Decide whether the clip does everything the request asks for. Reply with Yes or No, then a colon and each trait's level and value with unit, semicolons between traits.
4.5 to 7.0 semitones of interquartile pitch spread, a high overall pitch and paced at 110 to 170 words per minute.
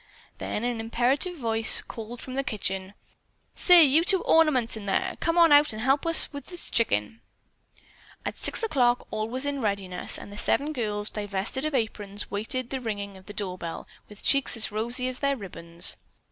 No: average, 5.2 semitones; high, 230 Hz; average, 185 wpm